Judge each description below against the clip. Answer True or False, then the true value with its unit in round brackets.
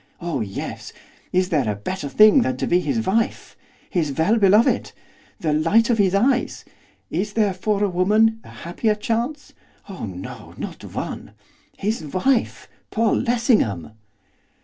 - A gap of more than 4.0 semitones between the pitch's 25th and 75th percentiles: True (5.0 semitones)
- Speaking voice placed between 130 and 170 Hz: False (200 Hz)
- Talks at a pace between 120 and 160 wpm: True (150 wpm)